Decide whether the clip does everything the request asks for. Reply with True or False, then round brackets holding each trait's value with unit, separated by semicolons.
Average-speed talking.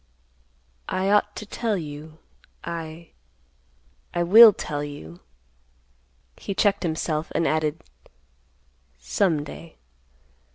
False (85 wpm)